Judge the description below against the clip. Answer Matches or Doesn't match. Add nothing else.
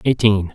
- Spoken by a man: Matches